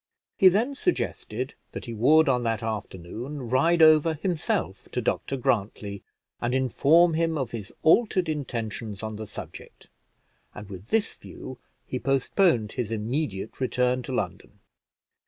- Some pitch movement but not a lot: No, wide, 6.2 semitones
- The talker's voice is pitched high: No, low, 130 Hz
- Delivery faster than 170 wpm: No, average, 140 wpm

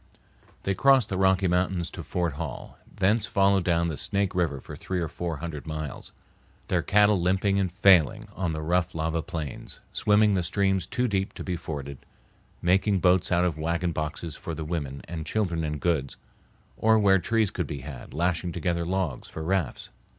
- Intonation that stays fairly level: No, average, 3.3 semitones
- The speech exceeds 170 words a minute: Yes, average, 185 wpm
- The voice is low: Yes, very low, 90 Hz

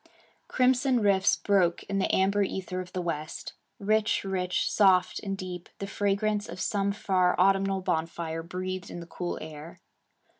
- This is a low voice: No, high, 190 Hz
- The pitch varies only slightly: Yes, narrow, 2.0 semitones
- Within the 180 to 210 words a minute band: No, average, 155 wpm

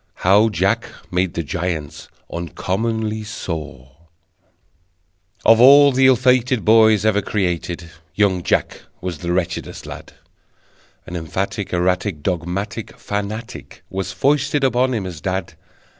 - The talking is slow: Yes, slow, 120 wpm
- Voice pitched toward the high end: No, very low, 95 Hz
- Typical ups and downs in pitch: Yes, average, 4.2 semitones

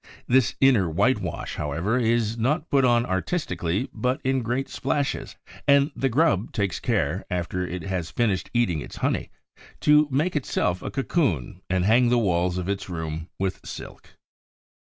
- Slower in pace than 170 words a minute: Yes, average, 155 wpm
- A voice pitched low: Yes, low, 110 Hz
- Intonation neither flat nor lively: No, wide, 6.4 semitones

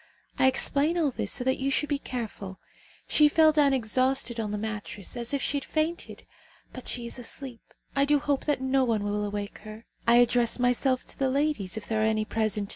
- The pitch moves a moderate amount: Yes, average, 4.3 semitones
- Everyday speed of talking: No, fast, 215 wpm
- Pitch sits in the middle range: No, very high, 250 Hz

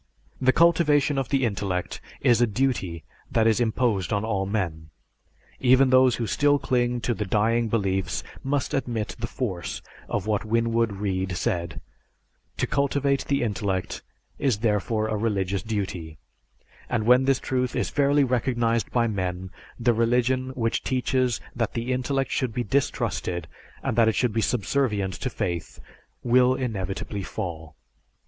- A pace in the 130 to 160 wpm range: Yes, average, 150 wpm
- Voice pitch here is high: No, low, 115 Hz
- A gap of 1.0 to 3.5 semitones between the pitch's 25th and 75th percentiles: No, average, 4.3 semitones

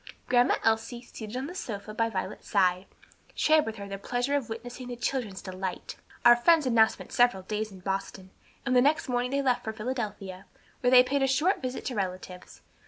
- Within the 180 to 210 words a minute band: Yes, fast, 205 wpm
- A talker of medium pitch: No, high, 235 Hz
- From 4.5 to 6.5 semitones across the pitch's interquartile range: No, average, 4.1 semitones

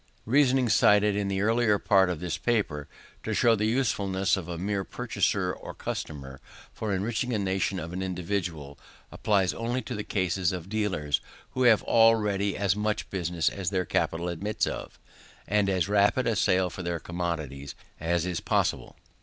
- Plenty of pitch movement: No, average, 3.4 semitones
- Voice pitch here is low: Yes, very low, 95 Hz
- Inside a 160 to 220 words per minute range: Yes, average, 175 wpm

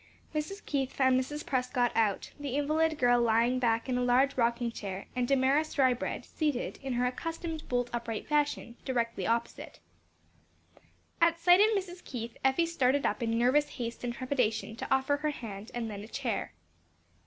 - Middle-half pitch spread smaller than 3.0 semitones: No, average, 3.8 semitones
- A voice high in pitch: Yes, very high, 255 Hz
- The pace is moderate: Yes, average, 170 wpm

